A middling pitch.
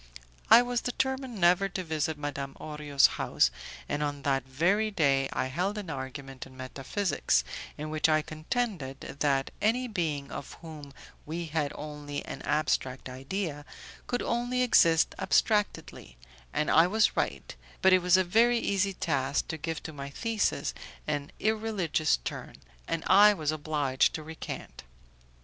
Yes: medium, 155 Hz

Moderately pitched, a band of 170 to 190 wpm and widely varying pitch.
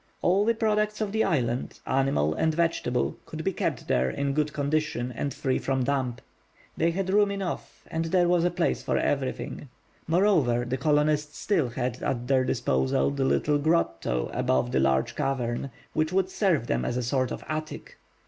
Yes: medium, 145 Hz; average, 180 wpm; wide, 5.8 semitones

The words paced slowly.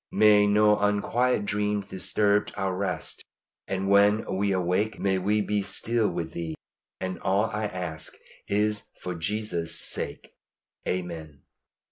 Yes: slow, 130 wpm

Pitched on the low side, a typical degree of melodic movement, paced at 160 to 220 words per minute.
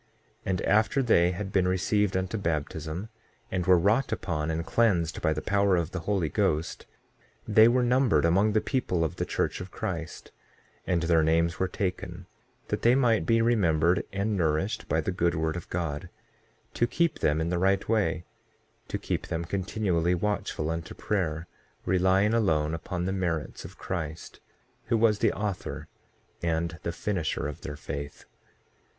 Yes: very low, 90 Hz; average, 4.0 semitones; average, 170 wpm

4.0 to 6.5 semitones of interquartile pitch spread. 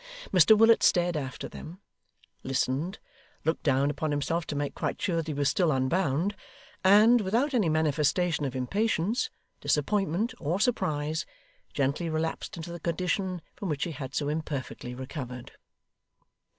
Yes: average, 4.6 semitones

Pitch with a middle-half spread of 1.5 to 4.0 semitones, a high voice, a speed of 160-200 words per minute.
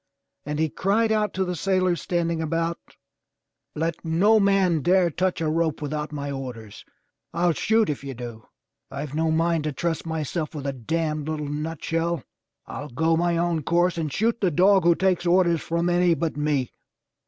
No: average, 2.9 semitones; medium, 165 Hz; average, 175 wpm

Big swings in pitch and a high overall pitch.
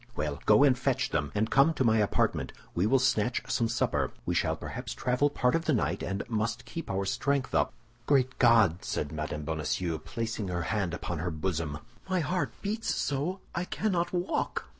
No: wide, 7.7 semitones; low, 115 Hz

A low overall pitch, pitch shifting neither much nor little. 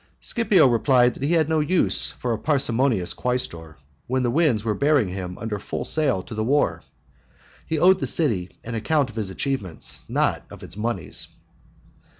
No: low, 125 Hz; wide, 5.8 semitones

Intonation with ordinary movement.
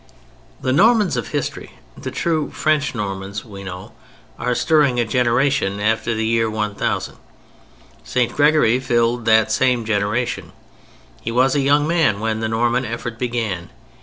Yes: average, 3.2 semitones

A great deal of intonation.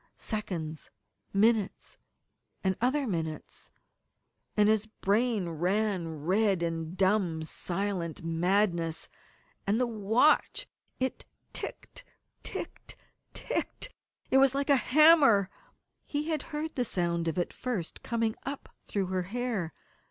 Yes: wide, 6.0 semitones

